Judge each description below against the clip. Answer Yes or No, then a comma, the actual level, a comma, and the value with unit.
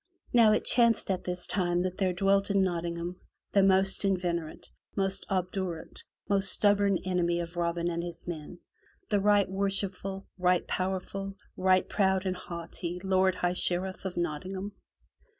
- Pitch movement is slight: Yes, narrow, 1.9 semitones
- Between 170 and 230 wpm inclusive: No, average, 150 wpm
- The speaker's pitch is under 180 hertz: No, medium, 185 Hz